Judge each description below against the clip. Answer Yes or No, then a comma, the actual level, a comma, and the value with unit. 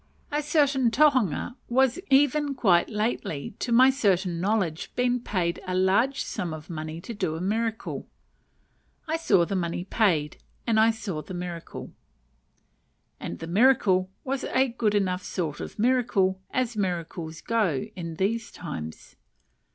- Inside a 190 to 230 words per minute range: No, average, 145 wpm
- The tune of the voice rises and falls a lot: Yes, wide, 6.1 semitones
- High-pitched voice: Yes, high, 200 Hz